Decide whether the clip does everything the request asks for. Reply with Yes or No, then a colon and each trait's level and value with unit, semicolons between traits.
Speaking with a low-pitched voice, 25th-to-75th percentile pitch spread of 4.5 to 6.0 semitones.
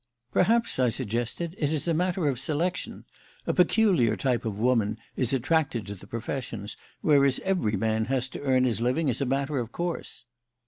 Yes: low, 130 Hz; wide, 5.4 semitones